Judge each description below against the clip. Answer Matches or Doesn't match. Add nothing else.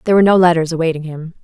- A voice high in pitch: Doesn't match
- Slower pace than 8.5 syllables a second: Doesn't match